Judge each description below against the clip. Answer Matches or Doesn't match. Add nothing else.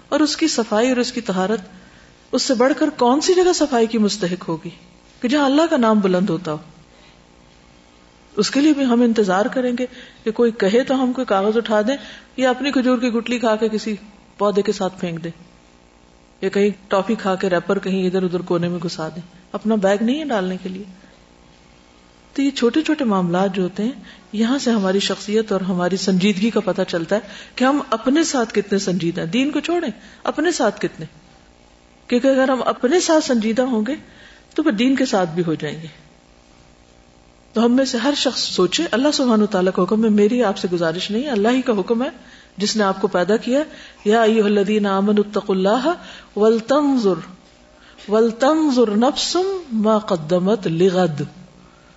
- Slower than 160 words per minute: Doesn't match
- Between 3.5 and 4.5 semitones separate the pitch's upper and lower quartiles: Doesn't match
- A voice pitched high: Matches